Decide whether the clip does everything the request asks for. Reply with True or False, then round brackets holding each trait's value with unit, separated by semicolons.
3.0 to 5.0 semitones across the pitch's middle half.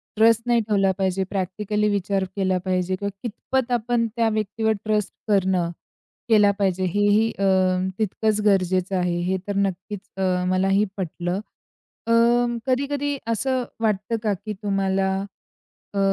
False (2.6 semitones)